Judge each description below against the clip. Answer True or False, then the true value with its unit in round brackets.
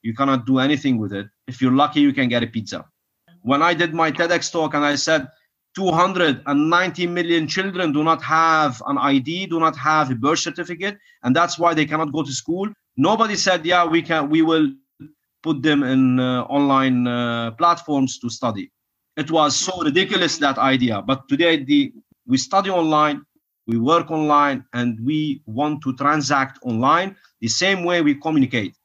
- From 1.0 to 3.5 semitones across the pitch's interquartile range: False (4.3 semitones)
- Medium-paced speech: True (180 wpm)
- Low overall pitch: False (150 Hz)